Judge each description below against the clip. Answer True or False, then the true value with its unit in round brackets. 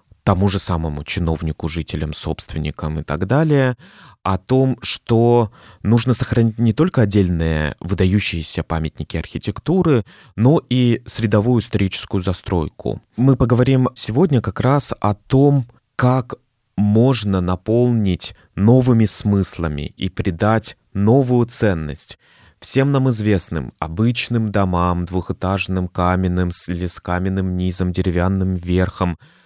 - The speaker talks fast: False (110 wpm)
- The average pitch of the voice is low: True (100 Hz)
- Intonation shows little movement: False (5.1 semitones)